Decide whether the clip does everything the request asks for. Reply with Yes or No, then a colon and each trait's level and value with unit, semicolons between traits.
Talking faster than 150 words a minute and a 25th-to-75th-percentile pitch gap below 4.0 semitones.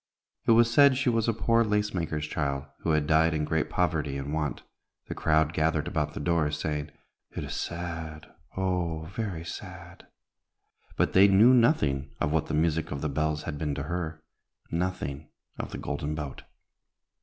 Yes: average, 180 wpm; average, 3.4 semitones